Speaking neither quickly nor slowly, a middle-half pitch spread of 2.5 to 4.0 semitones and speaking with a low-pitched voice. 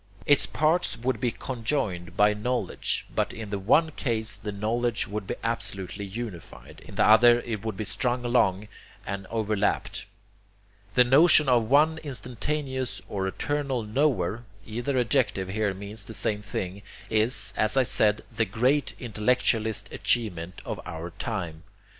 Yes: average, 145 wpm; average, 3.7 semitones; low, 110 Hz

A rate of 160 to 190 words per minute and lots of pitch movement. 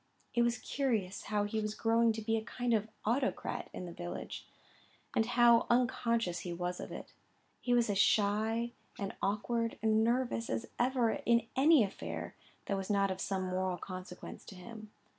No: average, 180 wpm; average, 3.2 semitones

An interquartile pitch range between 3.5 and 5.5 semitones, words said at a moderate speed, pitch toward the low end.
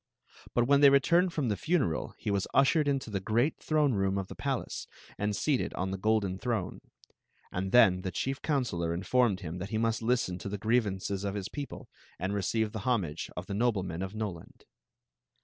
No: average, 4.8 semitones; fast, 220 wpm; low, 105 Hz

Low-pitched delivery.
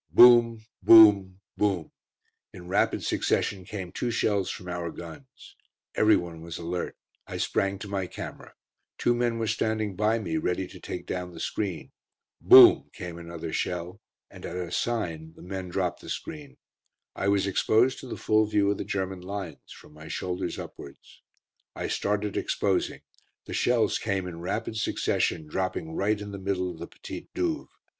Yes: very low, 95 Hz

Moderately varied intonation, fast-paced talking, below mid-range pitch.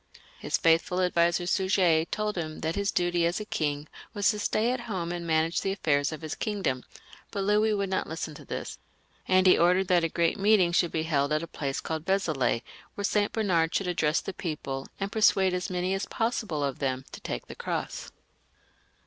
No: average, 3.7 semitones; fast, 210 wpm; medium, 175 Hz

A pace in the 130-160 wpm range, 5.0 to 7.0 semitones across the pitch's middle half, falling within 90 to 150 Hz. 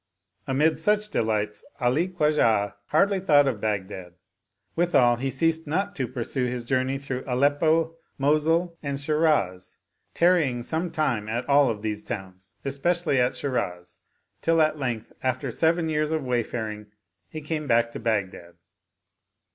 Yes: average, 145 wpm; wide, 5.4 semitones; low, 135 Hz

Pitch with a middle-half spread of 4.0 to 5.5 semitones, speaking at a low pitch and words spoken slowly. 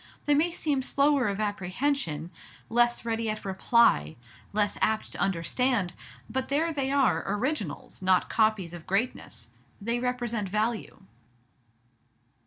No: average, 5.2 semitones; high, 225 Hz; slow, 125 wpm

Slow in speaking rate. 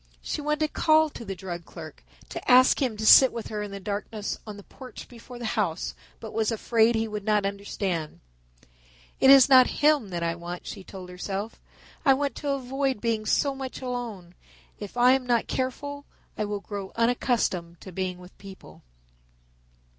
No: average, 185 wpm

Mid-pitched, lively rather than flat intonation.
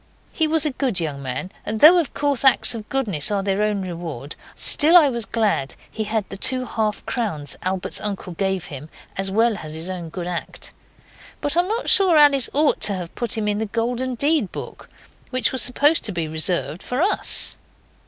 No: high, 215 Hz; wide, 7.0 semitones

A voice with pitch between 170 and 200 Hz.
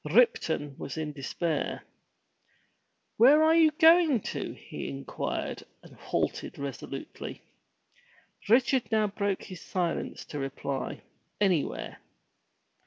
Yes: medium, 185 Hz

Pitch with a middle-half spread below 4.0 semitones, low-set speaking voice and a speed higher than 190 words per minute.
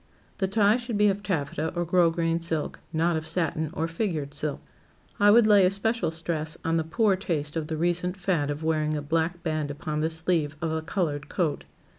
No: average, 2.9 semitones; medium, 165 Hz; average, 200 wpm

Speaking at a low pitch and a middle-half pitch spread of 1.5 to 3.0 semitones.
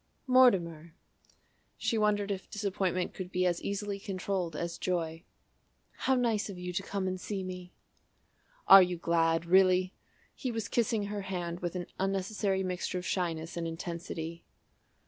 No: medium, 185 Hz; average, 2.7 semitones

